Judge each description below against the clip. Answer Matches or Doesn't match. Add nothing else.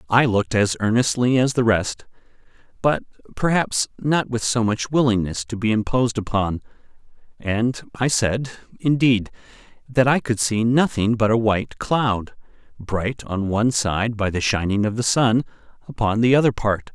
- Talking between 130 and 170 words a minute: Matches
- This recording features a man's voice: Matches